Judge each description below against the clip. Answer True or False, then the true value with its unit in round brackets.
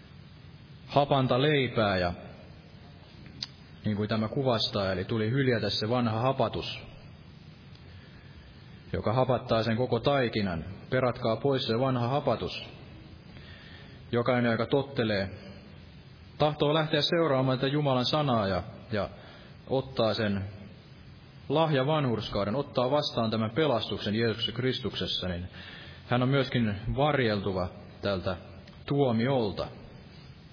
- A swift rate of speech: False (100 wpm)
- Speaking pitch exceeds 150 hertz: False (115 Hz)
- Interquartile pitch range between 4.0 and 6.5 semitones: True (4.7 semitones)